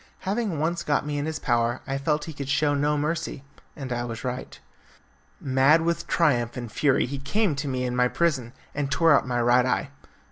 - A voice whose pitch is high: No, medium, 140 Hz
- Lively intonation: No, average, 3.5 semitones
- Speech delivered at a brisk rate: Yes, fast, 210 wpm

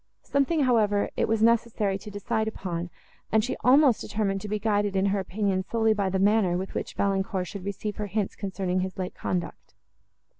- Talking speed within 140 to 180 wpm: No, average, 190 wpm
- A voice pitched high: Yes, high, 205 Hz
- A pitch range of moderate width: No, narrow, 2.3 semitones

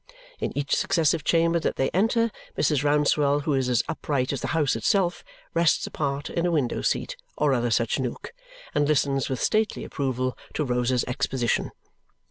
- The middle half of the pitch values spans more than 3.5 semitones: Yes, average, 4.2 semitones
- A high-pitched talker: No, medium, 145 Hz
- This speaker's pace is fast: No, average, 170 wpm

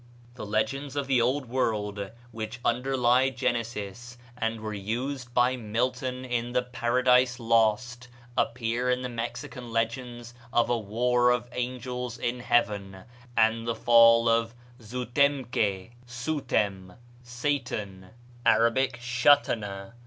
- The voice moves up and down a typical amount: No, narrow, 1.8 semitones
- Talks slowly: Yes, slow, 125 wpm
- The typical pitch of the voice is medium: No, low, 120 Hz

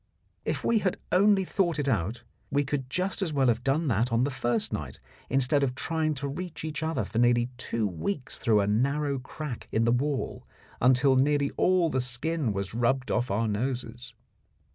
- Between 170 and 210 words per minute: Yes, average, 190 wpm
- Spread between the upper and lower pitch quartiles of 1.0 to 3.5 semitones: No, average, 4.1 semitones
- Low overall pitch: Yes, low, 130 Hz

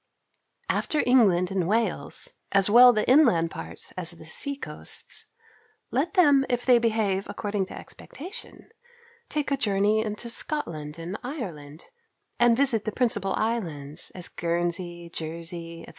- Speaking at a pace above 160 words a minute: No, average, 140 wpm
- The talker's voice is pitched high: Yes, high, 205 Hz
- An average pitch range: No, wide, 6.3 semitones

